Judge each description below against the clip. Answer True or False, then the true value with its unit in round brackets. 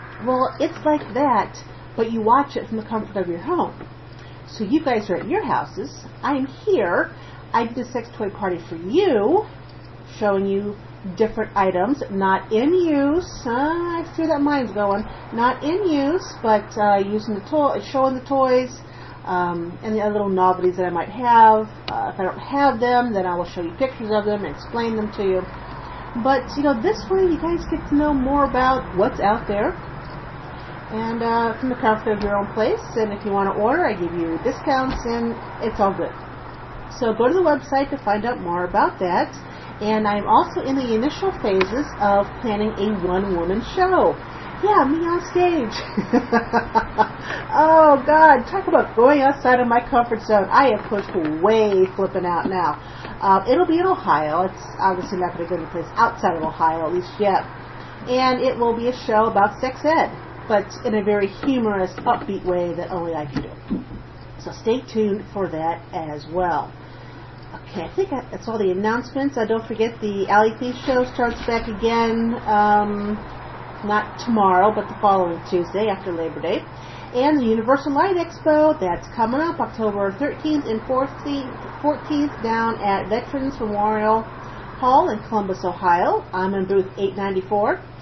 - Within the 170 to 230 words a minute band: True (180 wpm)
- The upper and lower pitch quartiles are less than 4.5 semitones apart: False (5.5 semitones)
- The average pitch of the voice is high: True (220 Hz)